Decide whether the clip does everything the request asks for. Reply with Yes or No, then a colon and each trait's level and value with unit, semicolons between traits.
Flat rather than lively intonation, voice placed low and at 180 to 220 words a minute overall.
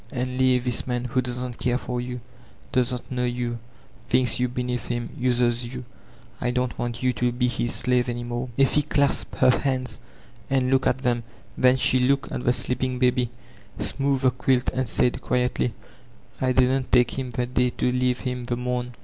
Yes: narrow, 0.8 semitones; low, 125 Hz; average, 190 wpm